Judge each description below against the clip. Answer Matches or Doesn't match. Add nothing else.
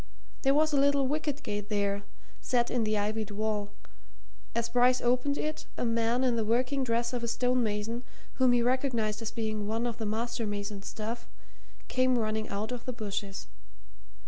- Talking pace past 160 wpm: Matches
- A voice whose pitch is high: Matches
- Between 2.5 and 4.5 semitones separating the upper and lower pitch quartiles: Matches